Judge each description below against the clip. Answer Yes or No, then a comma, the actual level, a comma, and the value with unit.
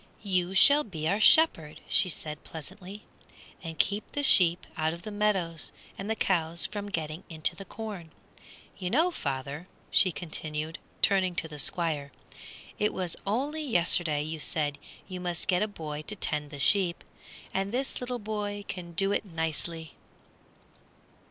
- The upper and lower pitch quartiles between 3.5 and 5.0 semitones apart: Yes, average, 4.3 semitones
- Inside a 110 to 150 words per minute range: No, average, 160 wpm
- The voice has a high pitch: No, medium, 180 Hz